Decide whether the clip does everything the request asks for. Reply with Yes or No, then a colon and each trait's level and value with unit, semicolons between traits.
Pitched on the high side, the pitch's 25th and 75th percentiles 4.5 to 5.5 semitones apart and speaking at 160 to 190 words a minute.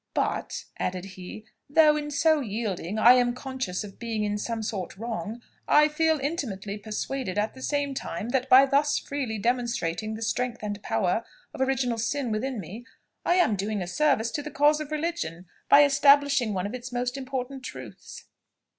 Yes: high, 245 Hz; average, 4.8 semitones; average, 180 wpm